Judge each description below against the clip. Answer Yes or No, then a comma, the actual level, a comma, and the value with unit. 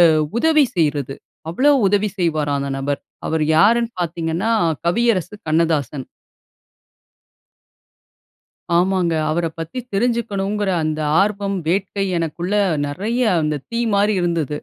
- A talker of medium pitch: Yes, medium, 175 Hz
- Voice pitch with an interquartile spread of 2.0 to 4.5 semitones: No, average, 4.9 semitones